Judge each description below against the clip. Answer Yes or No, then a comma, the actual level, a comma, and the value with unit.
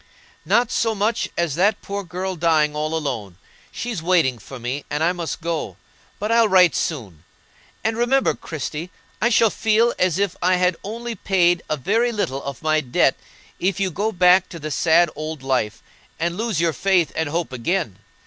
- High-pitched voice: No, medium, 175 Hz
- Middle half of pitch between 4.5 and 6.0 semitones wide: Yes, average, 4.8 semitones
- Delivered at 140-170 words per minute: No, average, 185 wpm